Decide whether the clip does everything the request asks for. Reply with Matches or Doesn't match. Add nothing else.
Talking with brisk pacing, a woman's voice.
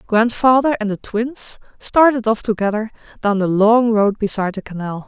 Doesn't match